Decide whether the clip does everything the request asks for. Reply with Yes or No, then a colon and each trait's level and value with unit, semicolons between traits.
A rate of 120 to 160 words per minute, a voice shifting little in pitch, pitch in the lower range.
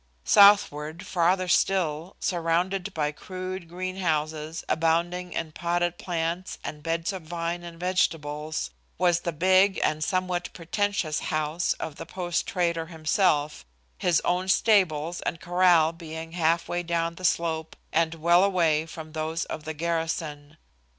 No: slow, 135 wpm; narrow, 2.2 semitones; medium, 170 Hz